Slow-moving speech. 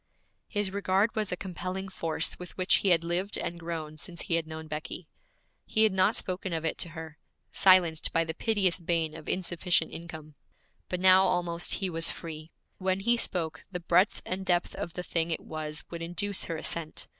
No: average, 195 wpm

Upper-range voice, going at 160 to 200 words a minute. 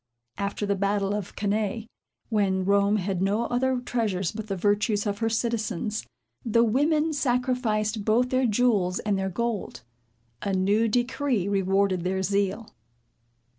No: high, 210 Hz; average, 140 wpm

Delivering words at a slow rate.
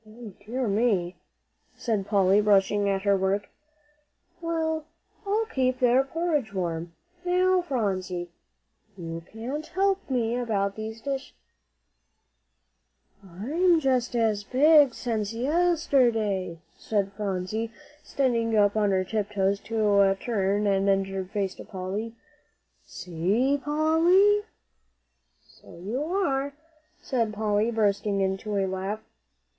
Yes: slow, 110 wpm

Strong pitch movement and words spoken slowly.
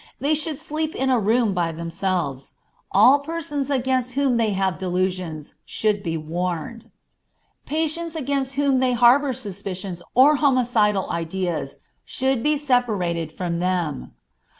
Yes: wide, 7.2 semitones; slow, 130 wpm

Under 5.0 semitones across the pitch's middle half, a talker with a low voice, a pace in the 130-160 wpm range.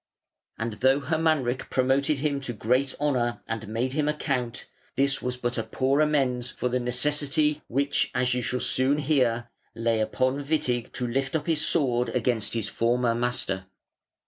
No: average, 2.8 semitones; low, 130 Hz; average, 170 wpm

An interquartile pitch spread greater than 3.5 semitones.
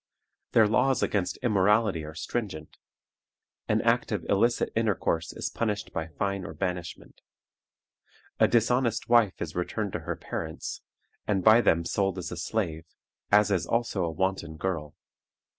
Yes: average, 4.7 semitones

